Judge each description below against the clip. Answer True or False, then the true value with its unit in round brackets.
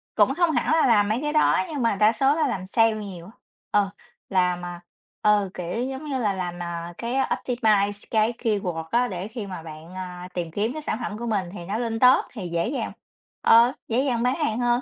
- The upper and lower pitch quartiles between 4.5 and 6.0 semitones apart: True (5.0 semitones)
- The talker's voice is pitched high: True (215 Hz)